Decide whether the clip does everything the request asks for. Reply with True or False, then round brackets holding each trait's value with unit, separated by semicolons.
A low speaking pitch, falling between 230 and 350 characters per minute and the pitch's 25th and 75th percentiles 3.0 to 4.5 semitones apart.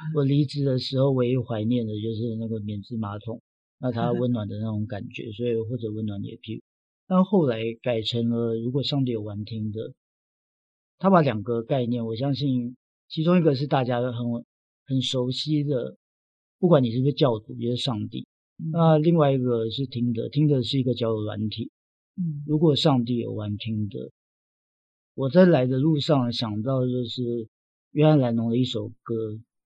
True (120 Hz; 265 characters per minute; 3.7 semitones)